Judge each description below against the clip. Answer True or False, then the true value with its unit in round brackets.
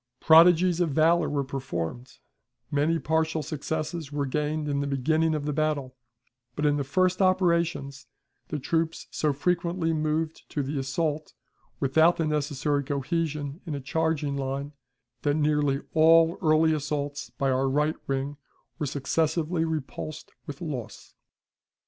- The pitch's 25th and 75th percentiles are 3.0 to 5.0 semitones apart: False (2.4 semitones)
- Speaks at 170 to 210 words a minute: False (140 wpm)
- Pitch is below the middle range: False (150 Hz)